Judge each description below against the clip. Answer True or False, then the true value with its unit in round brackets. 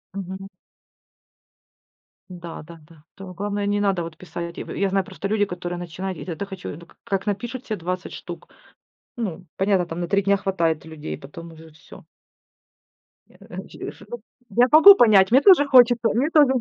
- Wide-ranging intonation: False (3.3 semitones)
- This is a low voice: False (190 Hz)